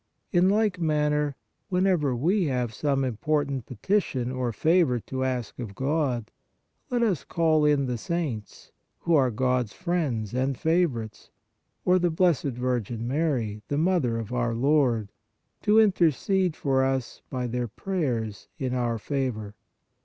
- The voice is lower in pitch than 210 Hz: Yes, low, 135 Hz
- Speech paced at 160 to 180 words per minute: No, average, 145 wpm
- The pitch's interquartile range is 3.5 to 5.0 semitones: No, wide, 5.4 semitones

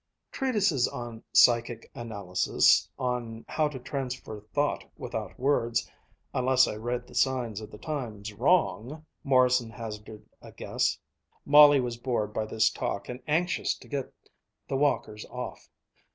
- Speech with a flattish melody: No, average, 3.8 semitones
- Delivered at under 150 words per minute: Yes, average, 140 wpm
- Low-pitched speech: Yes, low, 120 Hz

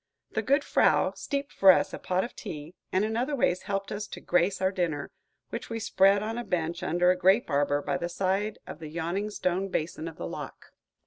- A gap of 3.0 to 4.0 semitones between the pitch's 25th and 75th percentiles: Yes, average, 3.6 semitones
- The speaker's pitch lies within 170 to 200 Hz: Yes, high, 190 Hz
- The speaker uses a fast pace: Yes, fast, 220 wpm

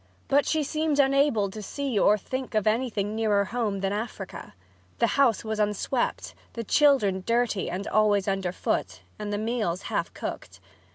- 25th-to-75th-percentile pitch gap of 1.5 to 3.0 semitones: No, average, 4.3 semitones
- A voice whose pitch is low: No, high, 215 Hz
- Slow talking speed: No, average, 165 wpm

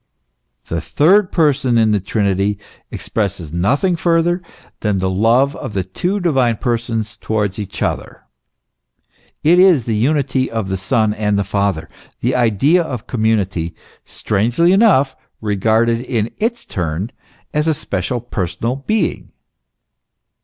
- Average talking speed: No, slow, 130 wpm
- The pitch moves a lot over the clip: Yes, wide, 6.1 semitones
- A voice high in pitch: No, low, 115 Hz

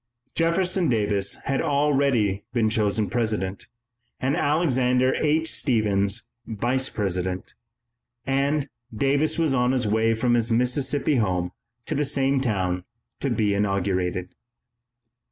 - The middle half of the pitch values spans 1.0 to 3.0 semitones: No, average, 5.3 semitones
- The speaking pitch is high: No, low, 120 Hz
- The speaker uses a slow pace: Yes, slow, 120 wpm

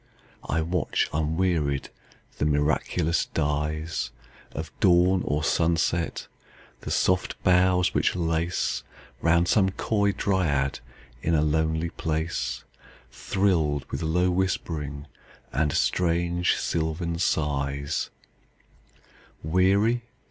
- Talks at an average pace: No, slow, 85 wpm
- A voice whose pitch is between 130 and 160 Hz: No, very low, 80 Hz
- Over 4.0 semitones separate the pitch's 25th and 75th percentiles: No, average, 3.2 semitones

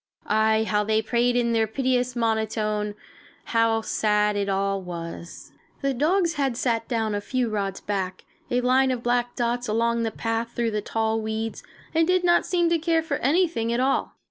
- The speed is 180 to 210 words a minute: Yes, average, 185 wpm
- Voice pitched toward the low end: No, high, 230 Hz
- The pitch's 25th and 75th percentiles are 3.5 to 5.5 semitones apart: No, average, 2.8 semitones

